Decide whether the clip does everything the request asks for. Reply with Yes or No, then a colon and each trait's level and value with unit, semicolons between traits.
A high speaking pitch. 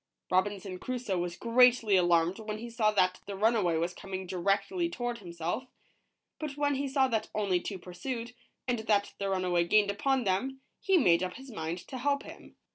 Yes: high, 205 Hz